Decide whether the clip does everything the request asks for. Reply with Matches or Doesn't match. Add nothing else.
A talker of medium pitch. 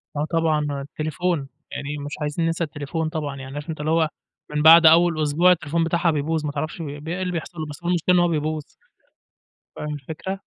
Matches